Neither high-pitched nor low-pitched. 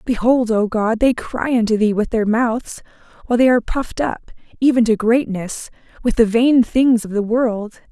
No: high, 230 Hz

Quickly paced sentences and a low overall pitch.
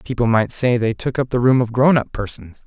Yes: fast, 270 wpm; low, 120 Hz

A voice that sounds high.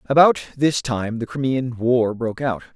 No: low, 125 Hz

